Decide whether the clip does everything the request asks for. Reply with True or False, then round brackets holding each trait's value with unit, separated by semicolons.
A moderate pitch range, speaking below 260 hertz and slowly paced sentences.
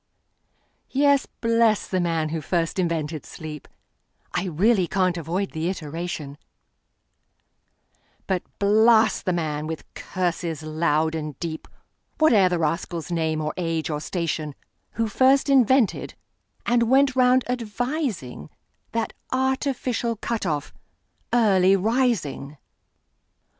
False (6.5 semitones; 185 Hz; 100 wpm)